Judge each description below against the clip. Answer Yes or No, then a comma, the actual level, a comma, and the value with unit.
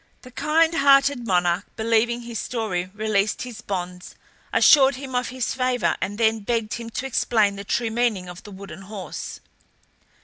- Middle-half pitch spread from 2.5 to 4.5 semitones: Yes, average, 4.0 semitones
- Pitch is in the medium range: No, high, 225 Hz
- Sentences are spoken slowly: No, average, 165 wpm